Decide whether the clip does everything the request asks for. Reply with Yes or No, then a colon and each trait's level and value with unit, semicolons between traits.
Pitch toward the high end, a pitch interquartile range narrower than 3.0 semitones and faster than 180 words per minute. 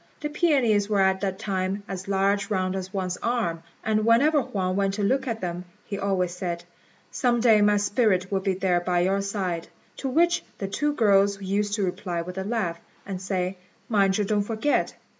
Yes: high, 200 Hz; narrow, 2.6 semitones; average, 195 wpm